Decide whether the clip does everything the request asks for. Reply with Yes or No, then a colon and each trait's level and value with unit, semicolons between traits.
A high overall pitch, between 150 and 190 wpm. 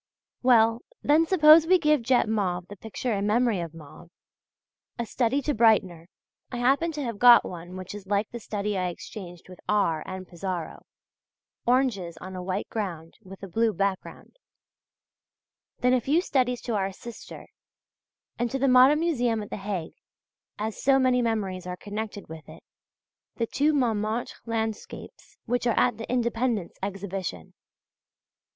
Yes: high, 220 Hz; average, 160 wpm